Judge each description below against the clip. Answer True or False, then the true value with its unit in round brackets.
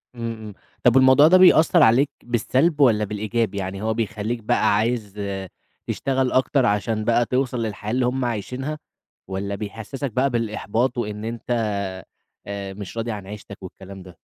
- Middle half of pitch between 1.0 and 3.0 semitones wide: False (3.5 semitones)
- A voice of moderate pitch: False (115 Hz)